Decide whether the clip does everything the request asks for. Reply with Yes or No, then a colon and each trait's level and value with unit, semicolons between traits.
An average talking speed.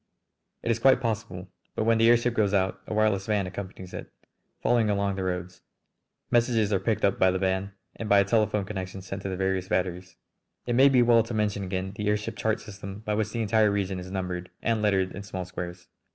No: fast, 220 wpm